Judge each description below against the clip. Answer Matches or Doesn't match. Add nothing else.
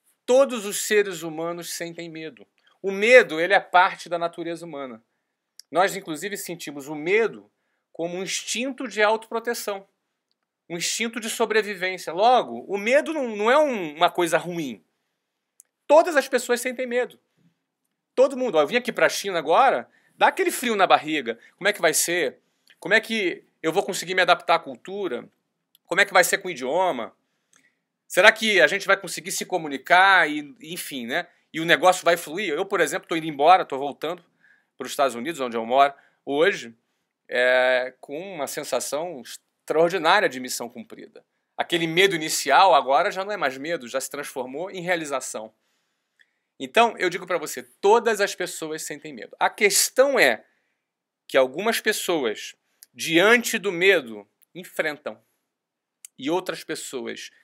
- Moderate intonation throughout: Doesn't match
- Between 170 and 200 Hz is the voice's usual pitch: Matches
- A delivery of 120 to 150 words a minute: Doesn't match